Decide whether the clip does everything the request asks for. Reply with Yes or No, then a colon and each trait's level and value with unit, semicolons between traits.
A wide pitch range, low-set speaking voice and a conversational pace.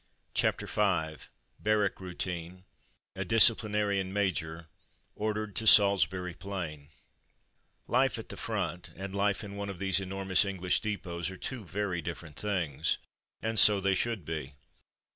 No: average, 2.9 semitones; very low, 95 Hz; average, 145 wpm